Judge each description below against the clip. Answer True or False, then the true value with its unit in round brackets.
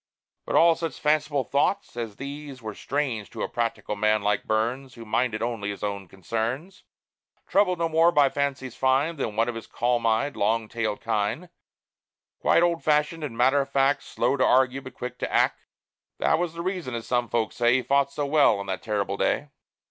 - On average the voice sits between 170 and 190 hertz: False (130 Hz)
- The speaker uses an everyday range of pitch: True (4.7 semitones)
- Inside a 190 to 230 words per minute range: True (200 wpm)